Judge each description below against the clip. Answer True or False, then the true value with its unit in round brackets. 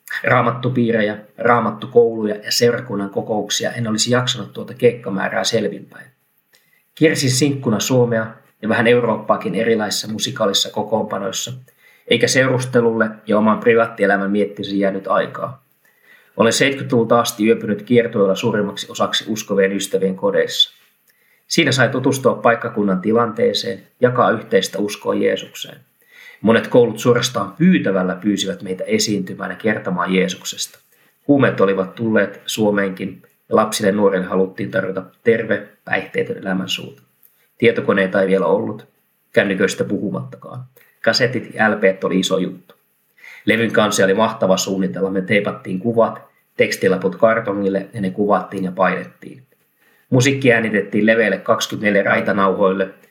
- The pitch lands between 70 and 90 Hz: False (105 Hz)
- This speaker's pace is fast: False (115 wpm)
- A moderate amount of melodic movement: True (3.6 semitones)